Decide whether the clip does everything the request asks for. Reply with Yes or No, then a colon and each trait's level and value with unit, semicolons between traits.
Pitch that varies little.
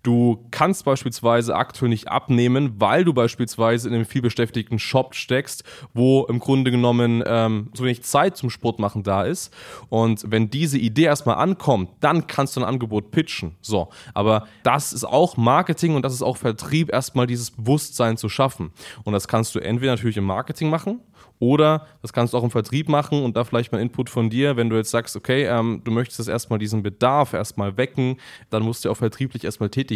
No: average, 3.0 semitones